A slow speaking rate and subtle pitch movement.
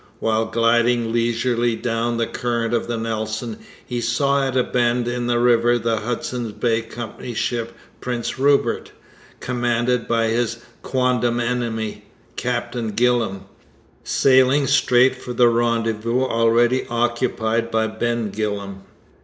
Yes: slow, 130 wpm; narrow, 1.3 semitones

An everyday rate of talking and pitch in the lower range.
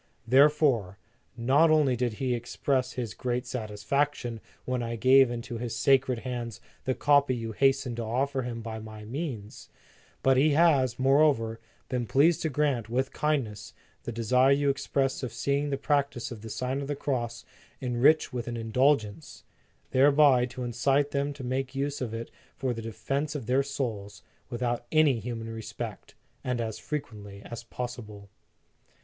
Yes: average, 165 wpm; low, 125 Hz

